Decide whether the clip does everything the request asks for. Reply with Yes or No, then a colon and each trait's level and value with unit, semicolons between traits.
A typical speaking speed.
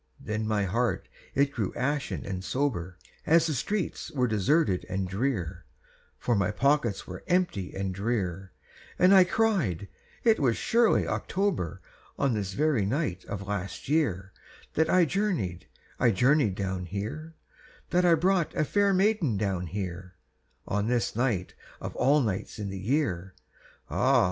Yes: average, 150 wpm